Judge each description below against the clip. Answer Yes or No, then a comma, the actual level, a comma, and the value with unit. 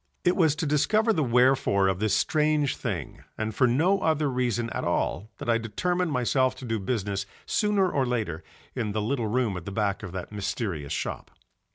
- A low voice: Yes, low, 120 Hz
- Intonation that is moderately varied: No, wide, 6.5 semitones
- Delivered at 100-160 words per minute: No, average, 195 wpm